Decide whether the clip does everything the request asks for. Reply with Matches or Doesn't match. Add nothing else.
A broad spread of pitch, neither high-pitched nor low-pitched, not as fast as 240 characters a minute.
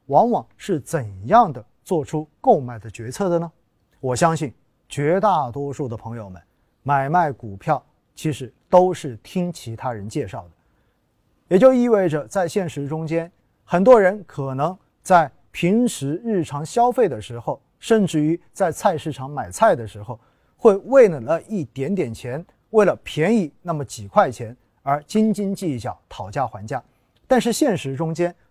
Matches